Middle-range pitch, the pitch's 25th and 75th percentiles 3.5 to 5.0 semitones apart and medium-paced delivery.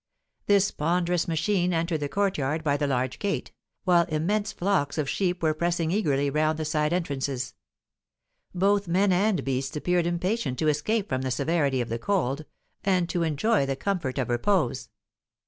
Yes: medium, 165 Hz; average, 4.7 semitones; average, 165 wpm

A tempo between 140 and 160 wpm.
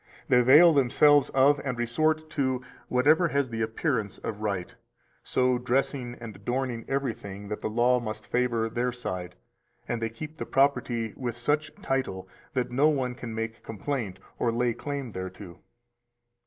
Yes: average, 155 wpm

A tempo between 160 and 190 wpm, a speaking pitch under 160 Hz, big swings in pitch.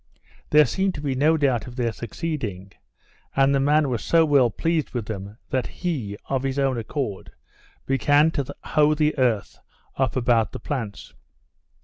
No: average, 165 wpm; low, 135 Hz; average, 4.3 semitones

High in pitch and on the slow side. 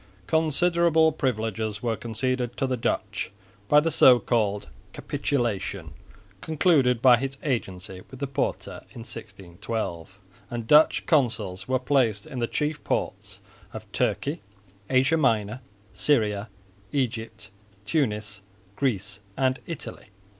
No: low, 120 Hz; slow, 120 wpm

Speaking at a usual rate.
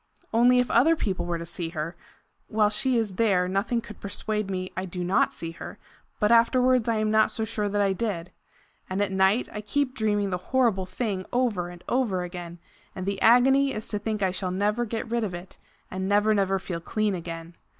No: fast, 210 wpm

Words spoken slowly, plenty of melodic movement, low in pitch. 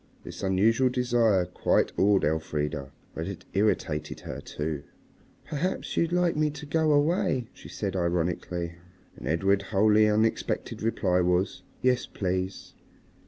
Yes: slow, 130 wpm; wide, 6.0 semitones; low, 100 Hz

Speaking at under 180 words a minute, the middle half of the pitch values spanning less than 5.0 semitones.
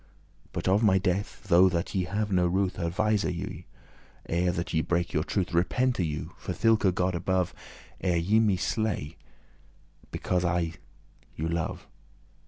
Yes: average, 160 wpm; average, 2.7 semitones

